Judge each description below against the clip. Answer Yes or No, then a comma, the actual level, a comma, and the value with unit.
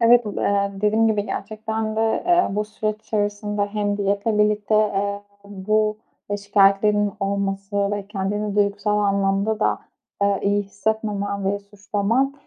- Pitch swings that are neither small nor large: No, narrow, 1.2 semitones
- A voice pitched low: No, high, 205 Hz